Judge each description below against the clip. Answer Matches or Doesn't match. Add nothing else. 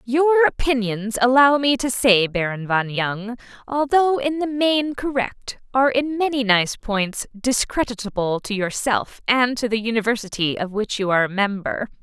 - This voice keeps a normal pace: Matches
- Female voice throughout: Matches